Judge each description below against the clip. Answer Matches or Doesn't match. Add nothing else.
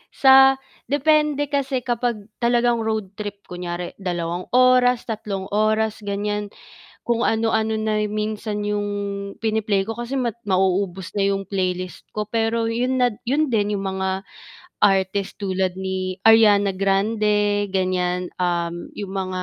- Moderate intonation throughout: Matches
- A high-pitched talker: Matches